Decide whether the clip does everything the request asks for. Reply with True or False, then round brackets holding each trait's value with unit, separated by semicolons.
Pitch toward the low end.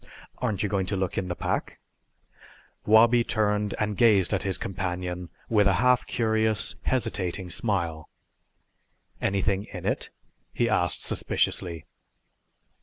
True (100 Hz)